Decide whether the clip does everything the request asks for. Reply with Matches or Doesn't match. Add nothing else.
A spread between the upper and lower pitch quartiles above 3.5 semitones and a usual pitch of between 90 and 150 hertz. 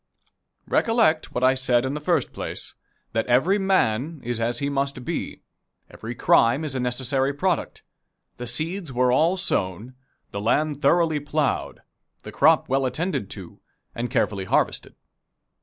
Matches